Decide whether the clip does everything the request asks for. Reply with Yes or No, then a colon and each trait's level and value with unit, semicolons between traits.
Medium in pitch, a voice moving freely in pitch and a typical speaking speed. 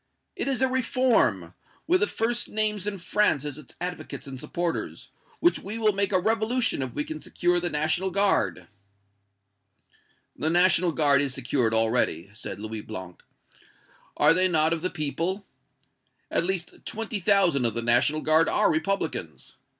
Yes: medium, 170 Hz; wide, 6.6 semitones; average, 160 wpm